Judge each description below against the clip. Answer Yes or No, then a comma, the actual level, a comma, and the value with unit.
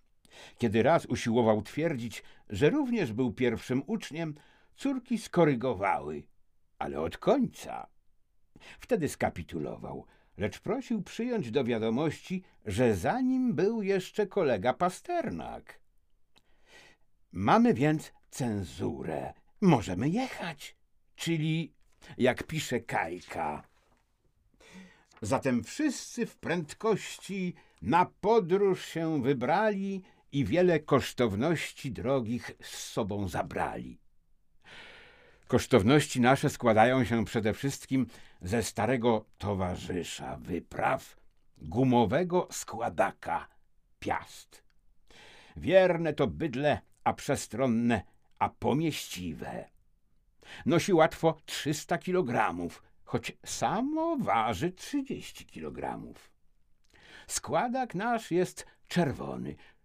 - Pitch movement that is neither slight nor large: No, wide, 8.0 semitones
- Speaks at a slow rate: Yes, slow, 85 wpm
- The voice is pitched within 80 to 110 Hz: No, medium, 140 Hz